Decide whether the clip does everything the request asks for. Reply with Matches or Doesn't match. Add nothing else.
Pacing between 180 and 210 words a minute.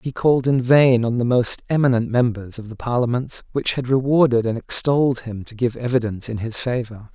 Matches